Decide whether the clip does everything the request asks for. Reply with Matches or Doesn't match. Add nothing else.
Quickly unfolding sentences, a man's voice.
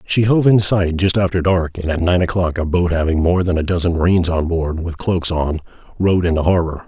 Matches